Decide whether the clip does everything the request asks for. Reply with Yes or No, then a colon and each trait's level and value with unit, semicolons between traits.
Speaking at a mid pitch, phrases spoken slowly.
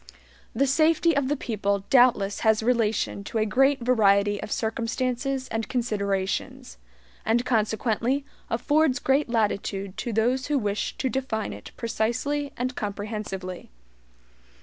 No: high, 230 Hz; slow, 125 wpm